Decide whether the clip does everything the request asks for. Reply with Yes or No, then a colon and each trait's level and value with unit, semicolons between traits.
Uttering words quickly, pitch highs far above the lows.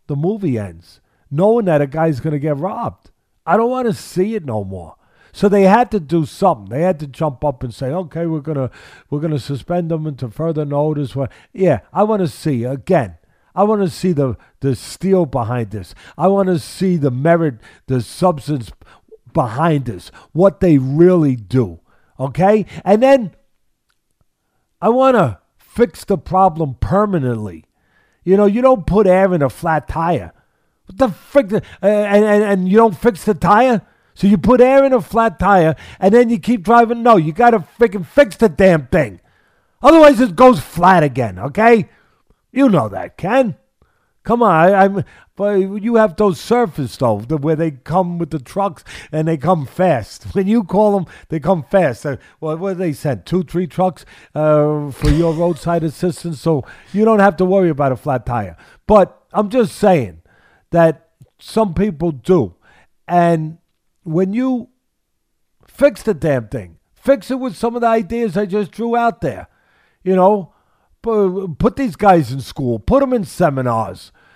No: average, 175 wpm; wide, 6.3 semitones